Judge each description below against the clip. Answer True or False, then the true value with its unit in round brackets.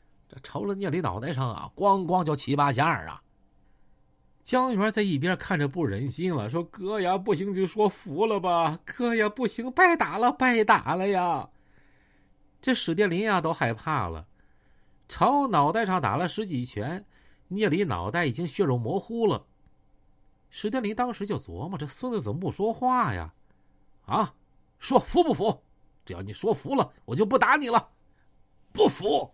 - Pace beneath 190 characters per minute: False (235 characters per minute)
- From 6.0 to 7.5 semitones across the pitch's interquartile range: True (6.4 semitones)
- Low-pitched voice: False (185 Hz)